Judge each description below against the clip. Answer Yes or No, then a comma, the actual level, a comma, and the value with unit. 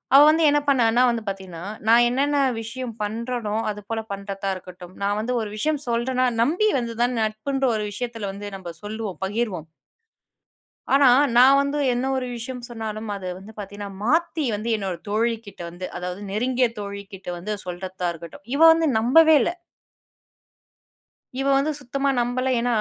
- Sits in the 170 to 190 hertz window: No, high, 225 Hz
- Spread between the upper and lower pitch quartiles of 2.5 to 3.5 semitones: No, average, 4.3 semitones